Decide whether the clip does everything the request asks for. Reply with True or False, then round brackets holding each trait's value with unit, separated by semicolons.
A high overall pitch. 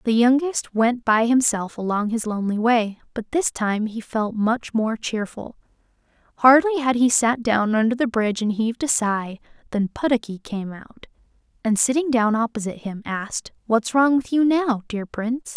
True (230 Hz)